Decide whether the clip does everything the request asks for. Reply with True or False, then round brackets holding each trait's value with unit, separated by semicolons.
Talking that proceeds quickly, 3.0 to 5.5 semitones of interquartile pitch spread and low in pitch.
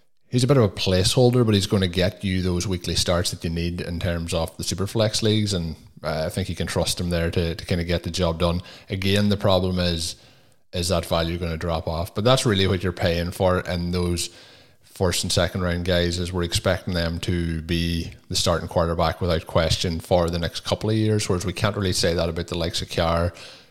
False (240 wpm; 2.4 semitones; 90 Hz)